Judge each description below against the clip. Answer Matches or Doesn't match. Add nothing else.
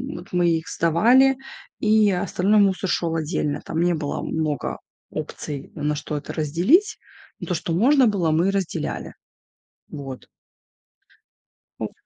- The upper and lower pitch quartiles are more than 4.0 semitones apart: Matches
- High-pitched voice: Doesn't match